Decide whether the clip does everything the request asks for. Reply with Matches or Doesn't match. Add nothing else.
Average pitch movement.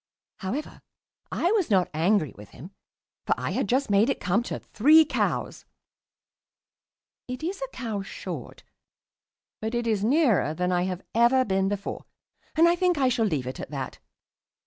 Doesn't match